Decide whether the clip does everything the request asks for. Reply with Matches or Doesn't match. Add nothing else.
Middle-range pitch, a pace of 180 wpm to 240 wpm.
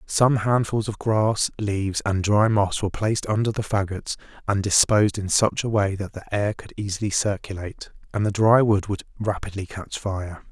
Doesn't match